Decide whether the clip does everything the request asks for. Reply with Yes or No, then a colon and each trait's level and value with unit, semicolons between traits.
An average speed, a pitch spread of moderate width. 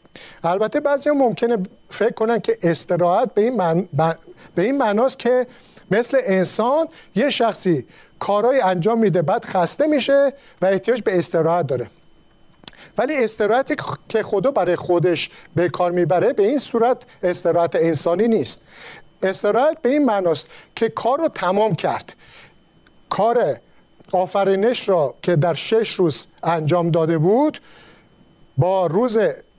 No: average, 135 wpm; wide, 5.7 semitones